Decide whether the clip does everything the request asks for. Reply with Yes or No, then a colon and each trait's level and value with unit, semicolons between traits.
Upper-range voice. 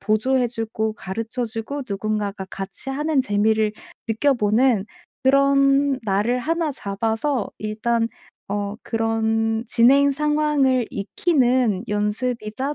Yes: high, 230 Hz